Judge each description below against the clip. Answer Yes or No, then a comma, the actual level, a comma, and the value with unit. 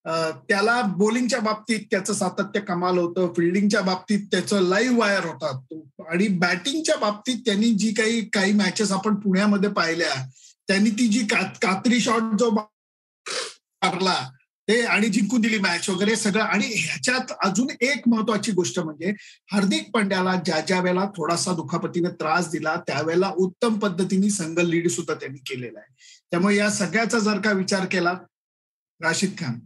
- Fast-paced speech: Yes, fast, 145 wpm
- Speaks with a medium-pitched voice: No, high, 200 Hz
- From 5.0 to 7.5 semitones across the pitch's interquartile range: No, average, 3.7 semitones